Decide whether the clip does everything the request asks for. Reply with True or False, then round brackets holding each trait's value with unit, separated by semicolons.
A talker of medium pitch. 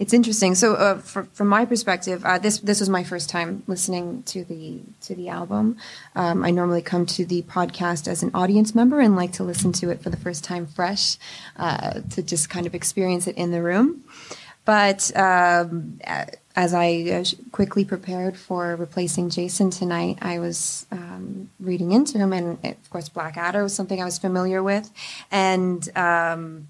True (180 Hz)